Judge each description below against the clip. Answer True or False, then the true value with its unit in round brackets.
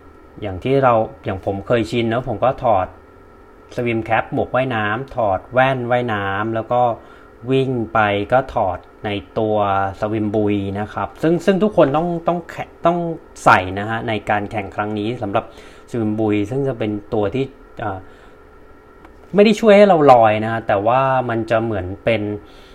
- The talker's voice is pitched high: False (115 Hz)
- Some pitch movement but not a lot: True (4.1 semitones)